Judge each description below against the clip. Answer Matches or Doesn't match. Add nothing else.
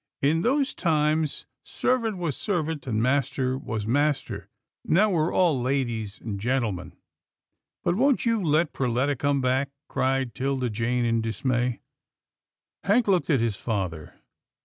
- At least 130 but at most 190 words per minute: Matches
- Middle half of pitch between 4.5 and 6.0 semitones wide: Matches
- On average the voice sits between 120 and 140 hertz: Matches